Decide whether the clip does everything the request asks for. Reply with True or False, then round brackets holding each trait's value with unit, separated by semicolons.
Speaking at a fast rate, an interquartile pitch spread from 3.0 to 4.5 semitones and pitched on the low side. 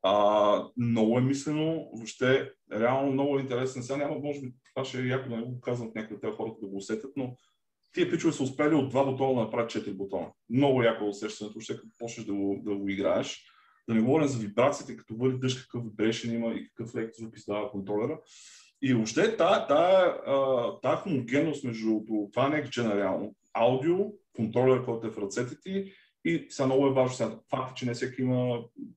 True (200 wpm; 3.6 semitones; 125 Hz)